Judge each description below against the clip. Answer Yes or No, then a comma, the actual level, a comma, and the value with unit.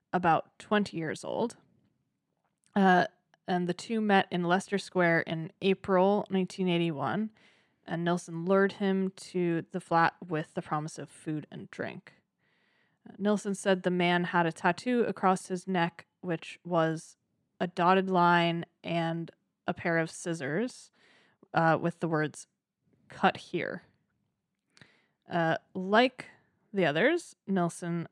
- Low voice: No, medium, 175 Hz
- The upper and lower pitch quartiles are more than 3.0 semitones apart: No, narrow, 2.6 semitones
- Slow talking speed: Yes, slow, 130 wpm